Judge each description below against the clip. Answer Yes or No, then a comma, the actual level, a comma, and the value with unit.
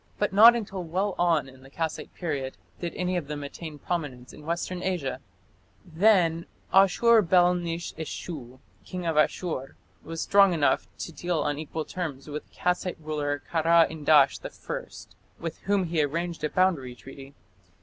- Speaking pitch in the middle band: Yes, medium, 165 Hz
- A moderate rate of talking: Yes, average, 160 wpm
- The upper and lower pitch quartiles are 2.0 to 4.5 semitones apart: Yes, average, 3.5 semitones